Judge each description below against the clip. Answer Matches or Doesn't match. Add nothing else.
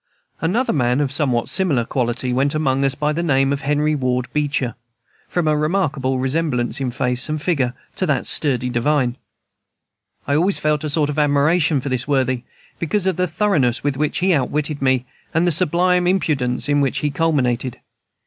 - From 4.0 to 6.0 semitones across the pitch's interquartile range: Doesn't match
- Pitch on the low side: Doesn't match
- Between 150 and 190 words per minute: Matches